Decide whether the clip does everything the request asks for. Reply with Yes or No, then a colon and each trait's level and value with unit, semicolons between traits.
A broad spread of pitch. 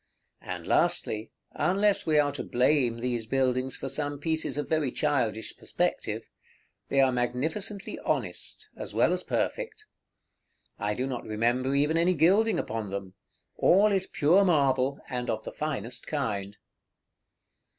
No: average, 4.7 semitones